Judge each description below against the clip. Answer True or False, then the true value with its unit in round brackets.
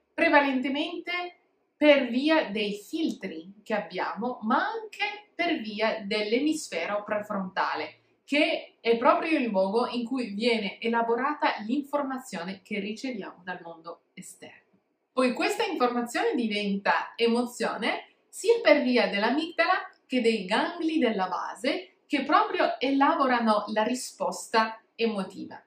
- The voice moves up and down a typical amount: False (6.6 semitones)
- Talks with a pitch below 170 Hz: False (250 Hz)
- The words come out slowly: True (110 wpm)